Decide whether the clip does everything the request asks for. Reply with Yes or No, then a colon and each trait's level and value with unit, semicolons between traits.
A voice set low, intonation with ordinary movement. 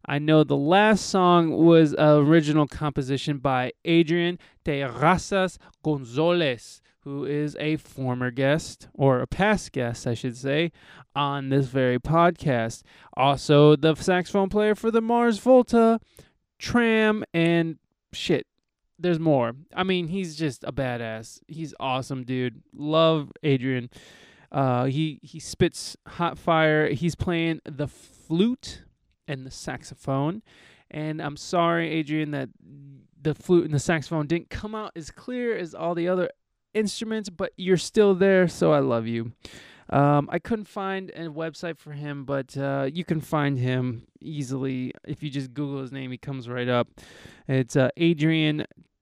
No: medium, 155 Hz; average, 4.0 semitones